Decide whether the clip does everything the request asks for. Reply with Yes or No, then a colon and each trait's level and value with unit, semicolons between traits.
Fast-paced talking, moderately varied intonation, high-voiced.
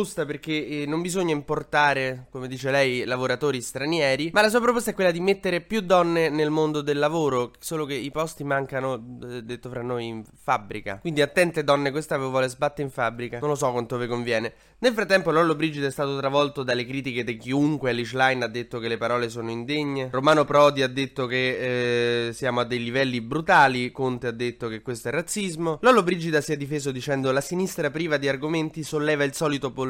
No: fast, 200 wpm; average, 3.9 semitones; medium, 140 Hz